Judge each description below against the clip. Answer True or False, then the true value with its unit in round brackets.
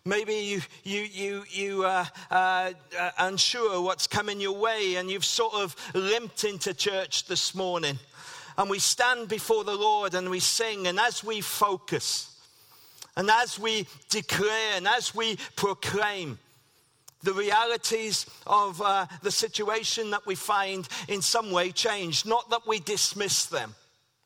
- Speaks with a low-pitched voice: False (200 Hz)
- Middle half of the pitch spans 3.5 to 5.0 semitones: False (2.9 semitones)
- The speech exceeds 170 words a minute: False (150 wpm)